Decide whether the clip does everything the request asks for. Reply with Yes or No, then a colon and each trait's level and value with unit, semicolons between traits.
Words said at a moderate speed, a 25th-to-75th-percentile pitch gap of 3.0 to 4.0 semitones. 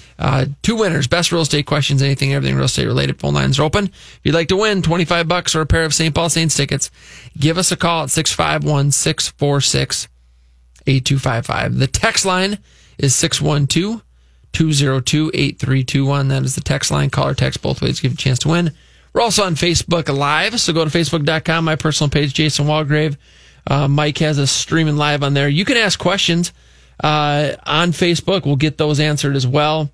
Yes: average, 195 wpm; average, 3.3 semitones